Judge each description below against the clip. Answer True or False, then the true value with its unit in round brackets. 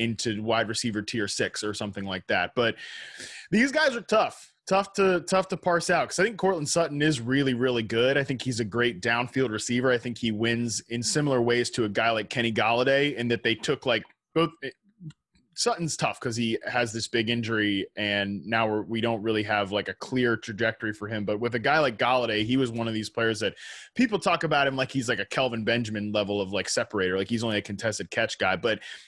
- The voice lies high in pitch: False (120 Hz)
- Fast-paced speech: True (230 wpm)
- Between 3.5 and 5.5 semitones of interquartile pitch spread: True (4.0 semitones)